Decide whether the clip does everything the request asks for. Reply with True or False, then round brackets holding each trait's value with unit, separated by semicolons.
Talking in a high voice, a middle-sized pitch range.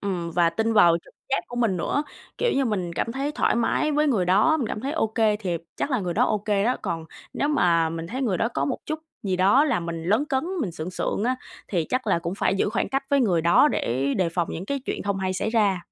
False (205 Hz; 6.7 semitones)